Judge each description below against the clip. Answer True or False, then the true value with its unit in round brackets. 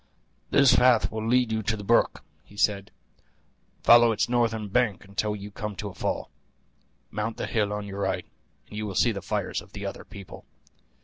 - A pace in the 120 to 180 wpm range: False (195 wpm)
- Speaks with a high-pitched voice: False (105 Hz)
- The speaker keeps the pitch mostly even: True (2.3 semitones)